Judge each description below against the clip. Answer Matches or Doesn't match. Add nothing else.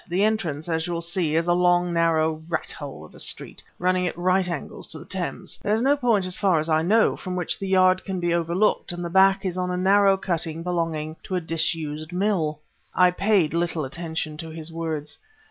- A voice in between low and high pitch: Matches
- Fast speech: Matches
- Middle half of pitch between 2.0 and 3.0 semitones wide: Matches